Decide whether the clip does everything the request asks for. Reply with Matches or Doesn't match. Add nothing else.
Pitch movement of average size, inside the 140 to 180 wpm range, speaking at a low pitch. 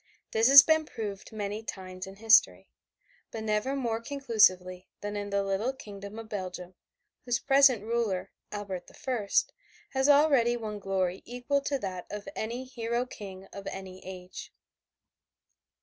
Doesn't match